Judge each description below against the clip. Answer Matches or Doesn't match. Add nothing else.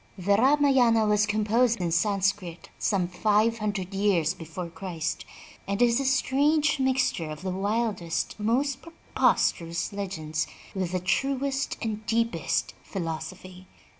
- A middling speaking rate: Doesn't match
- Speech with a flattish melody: Doesn't match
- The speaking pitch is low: Doesn't match